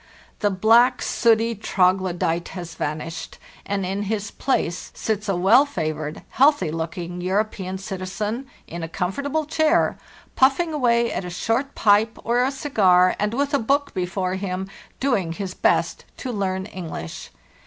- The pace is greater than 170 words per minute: No, average, 150 wpm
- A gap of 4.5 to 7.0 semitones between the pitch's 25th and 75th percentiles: Yes, average, 5.0 semitones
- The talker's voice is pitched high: Yes, high, 200 Hz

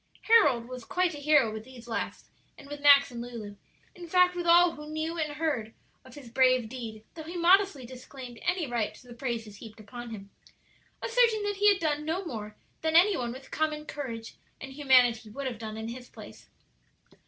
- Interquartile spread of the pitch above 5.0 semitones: Yes, wide, 5.5 semitones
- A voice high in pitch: Yes, very high, 265 Hz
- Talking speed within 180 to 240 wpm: Yes, average, 200 wpm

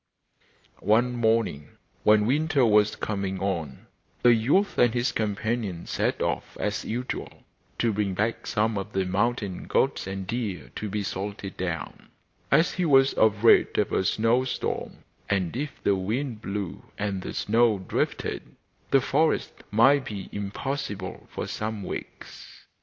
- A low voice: Yes, low, 105 Hz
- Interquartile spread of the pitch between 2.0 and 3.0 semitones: No, average, 3.8 semitones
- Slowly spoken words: No, average, 145 wpm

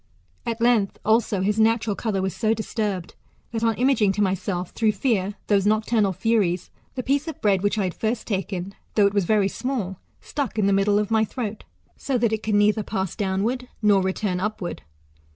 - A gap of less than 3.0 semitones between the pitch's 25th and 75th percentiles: Yes, narrow, 2.6 semitones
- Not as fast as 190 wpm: No, average, 200 wpm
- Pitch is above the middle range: Yes, high, 210 Hz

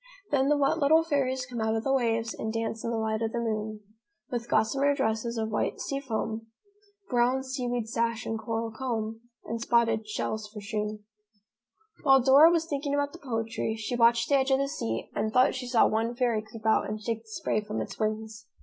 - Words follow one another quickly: Yes, fast, 210 wpm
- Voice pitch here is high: Yes, high, 230 Hz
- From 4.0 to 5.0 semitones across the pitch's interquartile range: No, average, 3.2 semitones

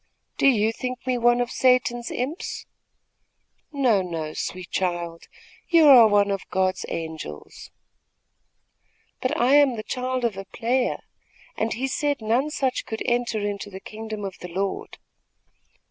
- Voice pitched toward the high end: Yes, high, 225 Hz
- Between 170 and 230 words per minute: No, average, 145 wpm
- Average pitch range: Yes, average, 4.6 semitones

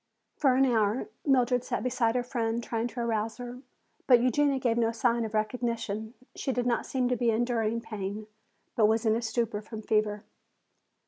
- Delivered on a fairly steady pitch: Yes, narrow, 2.1 semitones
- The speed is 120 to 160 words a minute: No, average, 185 wpm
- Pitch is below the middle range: No, high, 235 Hz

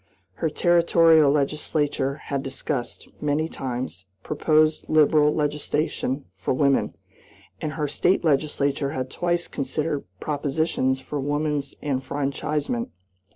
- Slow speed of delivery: Yes, slow, 105 wpm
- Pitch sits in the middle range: Yes, medium, 145 Hz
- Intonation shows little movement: Yes, narrow, 2.1 semitones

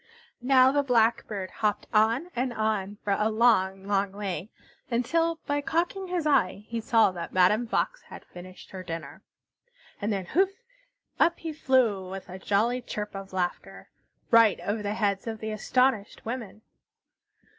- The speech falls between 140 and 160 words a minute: Yes, average, 155 wpm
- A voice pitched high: Yes, high, 220 Hz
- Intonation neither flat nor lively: Yes, average, 4.5 semitones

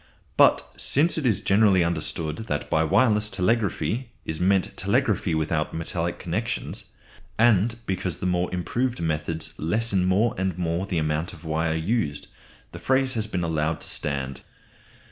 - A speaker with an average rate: Yes, average, 150 wpm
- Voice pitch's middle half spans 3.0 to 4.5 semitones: No, average, 5.2 semitones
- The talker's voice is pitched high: No, very low, 90 Hz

